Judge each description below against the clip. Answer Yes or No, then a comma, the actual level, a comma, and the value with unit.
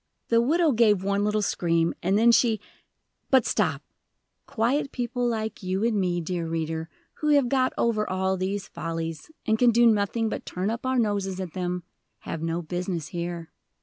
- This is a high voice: Yes, high, 200 Hz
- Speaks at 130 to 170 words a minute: No, average, 180 wpm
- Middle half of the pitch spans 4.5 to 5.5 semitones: Yes, average, 4.9 semitones